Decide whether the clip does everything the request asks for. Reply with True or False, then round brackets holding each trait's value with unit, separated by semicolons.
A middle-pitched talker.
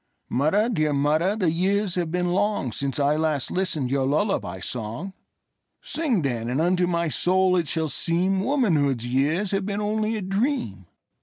True (175 Hz)